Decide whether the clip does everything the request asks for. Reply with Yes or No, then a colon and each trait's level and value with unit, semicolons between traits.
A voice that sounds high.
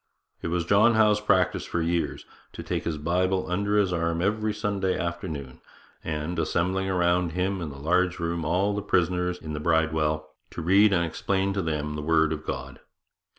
No: very low, 90 Hz